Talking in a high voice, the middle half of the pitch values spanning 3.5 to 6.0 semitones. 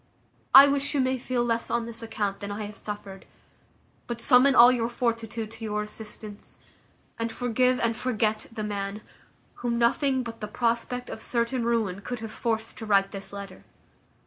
No: high, 230 Hz; narrow, 2.6 semitones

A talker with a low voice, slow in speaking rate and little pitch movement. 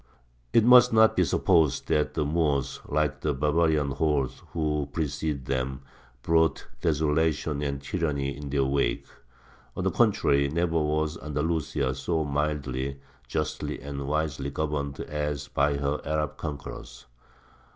Yes: very low, 75 Hz; slow, 130 wpm; narrow, 2.0 semitones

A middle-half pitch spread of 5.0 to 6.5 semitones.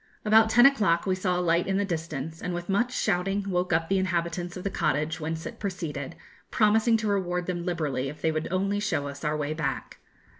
No: average, 3.6 semitones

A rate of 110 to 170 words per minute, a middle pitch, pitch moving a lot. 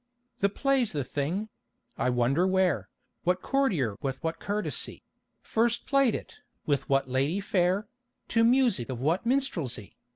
Yes: average, 140 wpm; medium, 180 Hz; wide, 8.7 semitones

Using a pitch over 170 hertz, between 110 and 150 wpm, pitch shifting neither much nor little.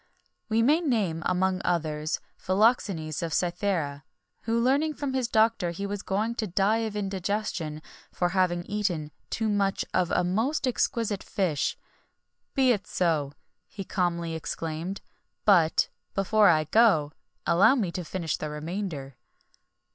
Yes: high, 190 Hz; average, 140 wpm; average, 4.7 semitones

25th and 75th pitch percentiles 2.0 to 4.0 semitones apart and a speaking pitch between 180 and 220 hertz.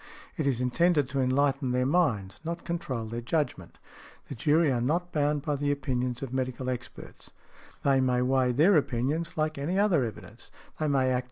No: average, 3.5 semitones; low, 135 Hz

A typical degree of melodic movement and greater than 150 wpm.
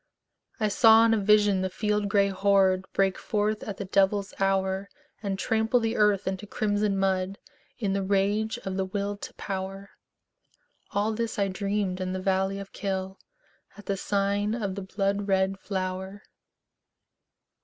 No: narrow, 1.4 semitones; average, 160 wpm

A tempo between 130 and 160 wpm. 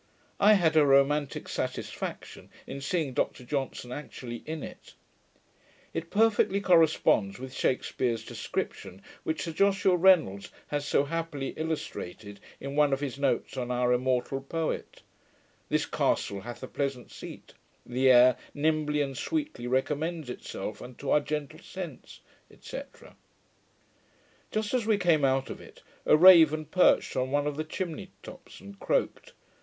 Yes: average, 145 wpm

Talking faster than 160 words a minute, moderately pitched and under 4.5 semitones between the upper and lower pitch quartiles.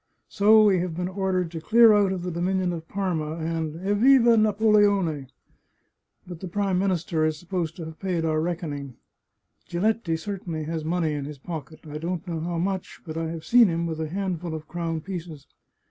Yes: average, 190 wpm; medium, 175 Hz; average, 3.2 semitones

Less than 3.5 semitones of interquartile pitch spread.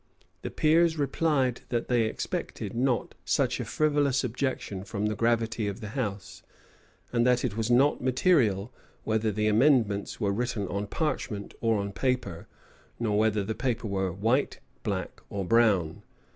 No: average, 4.0 semitones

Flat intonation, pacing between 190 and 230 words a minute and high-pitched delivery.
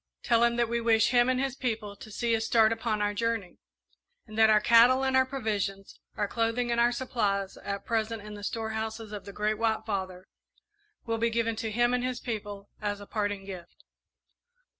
Yes: narrow, 2.3 semitones; fast, 205 wpm; high, 225 Hz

